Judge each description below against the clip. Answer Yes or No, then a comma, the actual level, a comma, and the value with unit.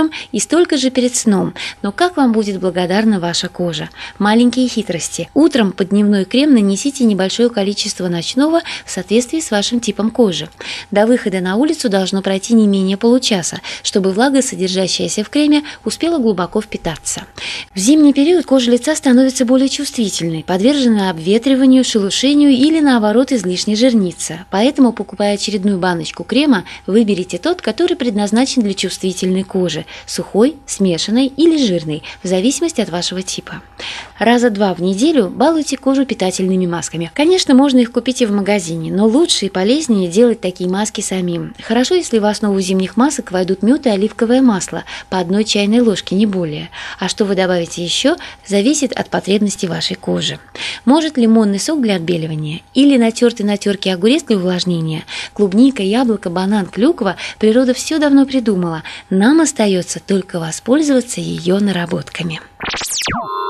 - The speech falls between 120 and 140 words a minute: No, average, 150 wpm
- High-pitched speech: Yes, high, 210 Hz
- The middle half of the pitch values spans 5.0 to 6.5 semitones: Yes, wide, 5.6 semitones